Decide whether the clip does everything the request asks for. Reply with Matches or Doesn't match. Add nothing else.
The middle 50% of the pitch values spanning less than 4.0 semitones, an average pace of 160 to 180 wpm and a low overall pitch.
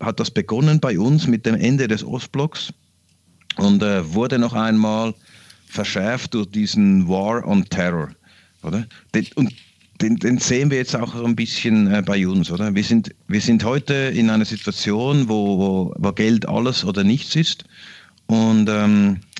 Doesn't match